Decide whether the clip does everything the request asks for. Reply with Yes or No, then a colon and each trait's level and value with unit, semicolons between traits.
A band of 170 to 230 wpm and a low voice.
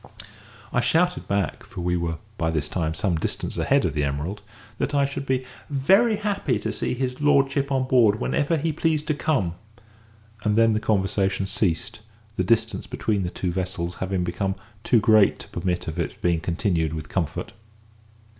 Yes: average, 175 wpm; low, 100 Hz